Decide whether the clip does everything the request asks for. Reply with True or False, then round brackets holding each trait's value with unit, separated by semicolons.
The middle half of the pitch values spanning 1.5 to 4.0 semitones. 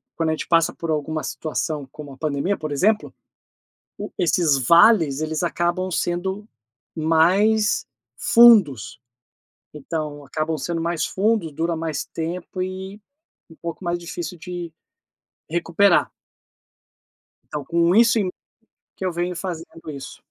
True (2.8 semitones)